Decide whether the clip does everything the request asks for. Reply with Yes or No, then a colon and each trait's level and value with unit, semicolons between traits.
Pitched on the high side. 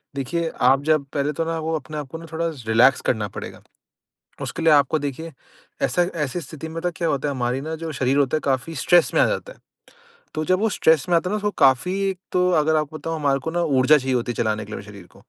No: medium, 150 Hz